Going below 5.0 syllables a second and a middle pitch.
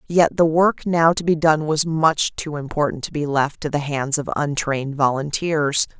Yes: 4.6 syllables/s; medium, 150 Hz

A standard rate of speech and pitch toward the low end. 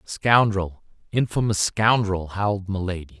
No: slow, 95 wpm; low, 100 Hz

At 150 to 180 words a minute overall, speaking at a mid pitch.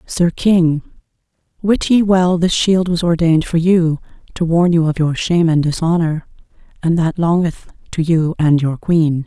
Yes: average, 175 wpm; medium, 165 Hz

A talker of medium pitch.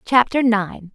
No: high, 225 Hz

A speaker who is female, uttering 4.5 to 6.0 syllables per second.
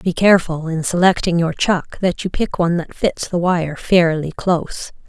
Yes: female; 4.7 syllables/s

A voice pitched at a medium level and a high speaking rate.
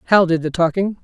Yes: medium, 175 Hz; fast, 230 wpm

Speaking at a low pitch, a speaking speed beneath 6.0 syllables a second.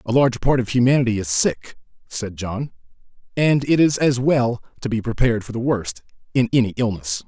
Yes: low, 120 Hz; 5.5 syllables/s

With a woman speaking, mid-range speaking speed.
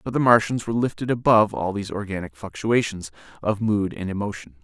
No: male; average, 180 wpm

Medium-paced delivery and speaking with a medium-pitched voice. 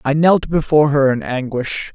Yes: average, 185 wpm; medium, 145 Hz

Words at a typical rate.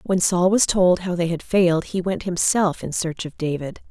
No: fast, 230 wpm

